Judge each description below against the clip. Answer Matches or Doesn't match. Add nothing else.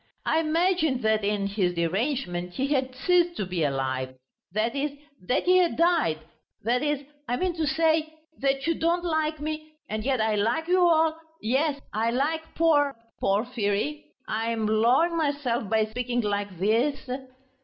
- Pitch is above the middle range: Matches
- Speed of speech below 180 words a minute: Matches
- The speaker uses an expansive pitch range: Matches